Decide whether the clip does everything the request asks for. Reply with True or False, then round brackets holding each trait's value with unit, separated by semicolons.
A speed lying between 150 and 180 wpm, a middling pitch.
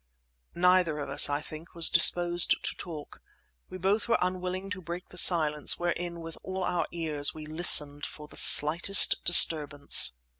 True (160 wpm; 170 Hz)